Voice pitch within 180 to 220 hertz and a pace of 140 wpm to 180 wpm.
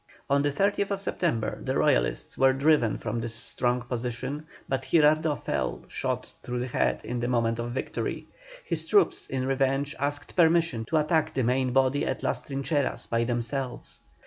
No: low, 135 Hz; average, 170 wpm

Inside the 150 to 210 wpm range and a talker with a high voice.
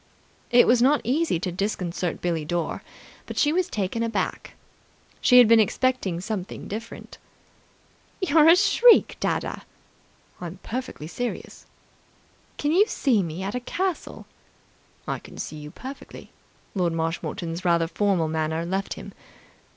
No: slow, 135 wpm; high, 205 Hz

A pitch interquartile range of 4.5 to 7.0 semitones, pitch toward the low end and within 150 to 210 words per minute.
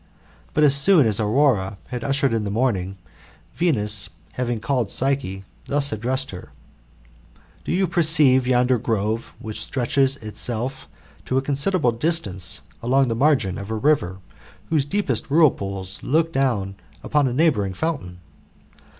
No: average, 5.2 semitones; low, 125 Hz; average, 140 wpm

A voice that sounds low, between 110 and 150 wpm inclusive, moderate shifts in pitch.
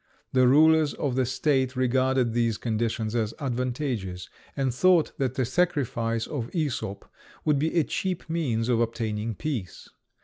Yes: low, 130 Hz; average, 145 wpm; average, 4.2 semitones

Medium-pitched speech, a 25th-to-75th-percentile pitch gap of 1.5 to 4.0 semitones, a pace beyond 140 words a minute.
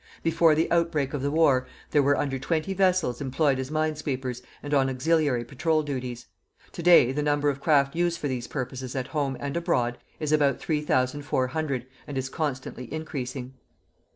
Yes: medium, 145 Hz; average, 3.2 semitones; average, 170 wpm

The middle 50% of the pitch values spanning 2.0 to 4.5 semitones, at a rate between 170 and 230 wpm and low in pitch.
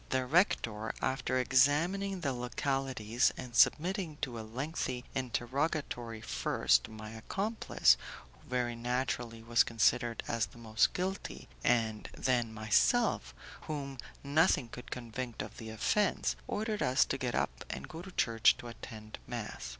No: average, 4.1 semitones; average, 140 wpm; low, 125 Hz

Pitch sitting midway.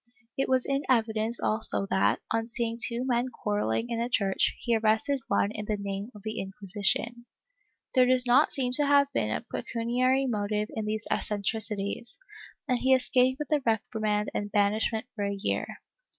No: high, 230 Hz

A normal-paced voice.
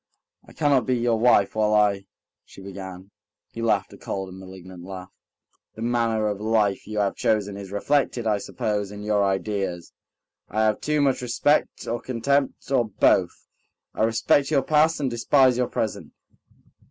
Yes: average, 165 wpm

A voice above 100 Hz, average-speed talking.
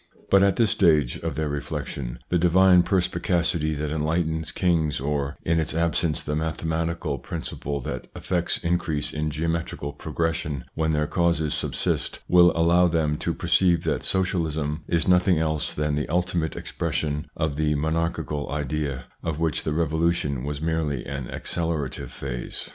No: very low, 80 Hz; average, 155 wpm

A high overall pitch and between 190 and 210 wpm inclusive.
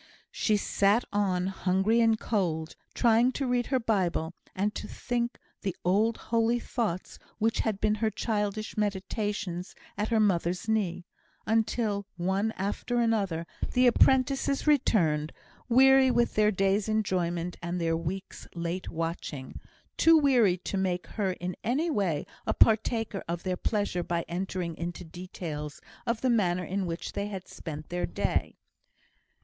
No: high, 200 Hz; average, 145 wpm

